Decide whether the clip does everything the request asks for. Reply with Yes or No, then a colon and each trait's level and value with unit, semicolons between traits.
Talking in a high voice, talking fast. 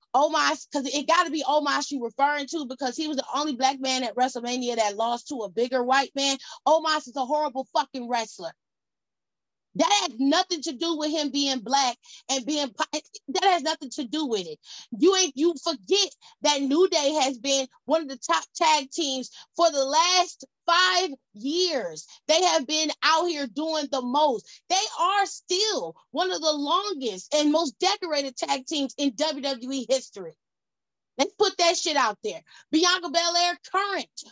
No: very high, 300 Hz; average, 180 wpm